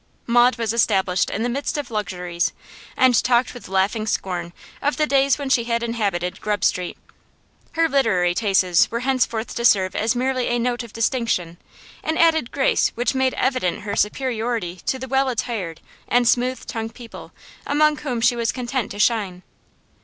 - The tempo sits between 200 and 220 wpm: No, average, 170 wpm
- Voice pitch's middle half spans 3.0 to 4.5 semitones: Yes, average, 4.2 semitones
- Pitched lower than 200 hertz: No, high, 235 Hz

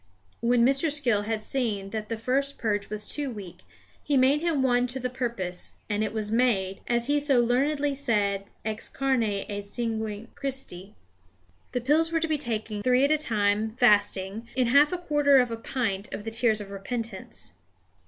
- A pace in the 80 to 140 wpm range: No, average, 185 wpm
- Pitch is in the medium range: No, high, 235 Hz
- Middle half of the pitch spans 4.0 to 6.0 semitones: Yes, average, 4.4 semitones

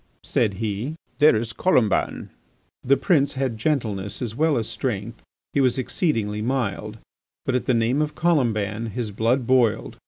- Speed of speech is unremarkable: Yes, average, 155 wpm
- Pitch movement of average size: Yes, average, 4.0 semitones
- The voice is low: Yes, low, 115 Hz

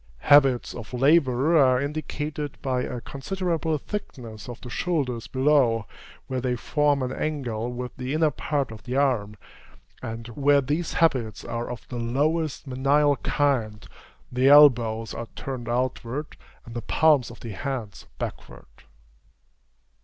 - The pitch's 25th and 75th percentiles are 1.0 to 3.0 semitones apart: No, average, 3.7 semitones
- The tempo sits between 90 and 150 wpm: Yes, average, 140 wpm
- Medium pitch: No, low, 130 Hz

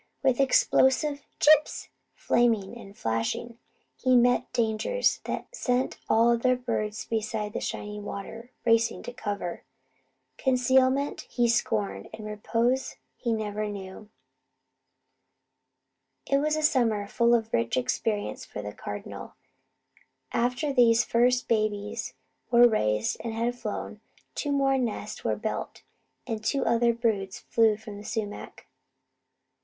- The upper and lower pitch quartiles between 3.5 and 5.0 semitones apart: No, average, 3.0 semitones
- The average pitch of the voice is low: No, high, 230 Hz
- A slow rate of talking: Yes, slow, 130 wpm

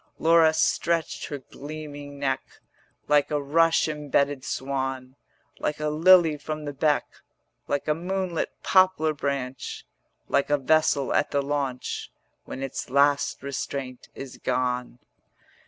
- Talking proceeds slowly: Yes, slow, 130 wpm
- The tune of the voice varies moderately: No, narrow, 2.3 semitones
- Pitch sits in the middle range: Yes, medium, 145 Hz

